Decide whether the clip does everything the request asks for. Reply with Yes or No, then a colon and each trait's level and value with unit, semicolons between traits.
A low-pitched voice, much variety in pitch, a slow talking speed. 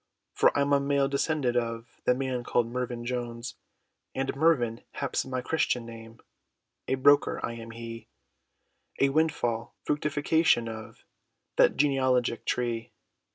No: low, 125 Hz; average, 3.0 semitones; slow, 130 wpm